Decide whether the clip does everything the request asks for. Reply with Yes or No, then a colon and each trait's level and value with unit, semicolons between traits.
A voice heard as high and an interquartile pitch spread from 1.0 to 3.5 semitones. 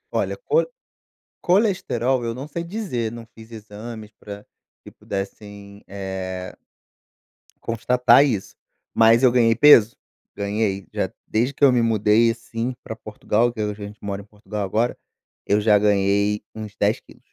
No: low, 110 Hz; average, 2.7 semitones